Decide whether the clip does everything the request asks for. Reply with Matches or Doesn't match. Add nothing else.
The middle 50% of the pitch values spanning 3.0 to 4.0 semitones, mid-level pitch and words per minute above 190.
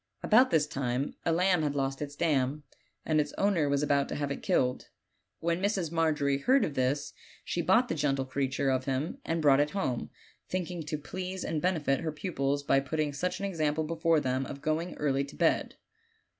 Matches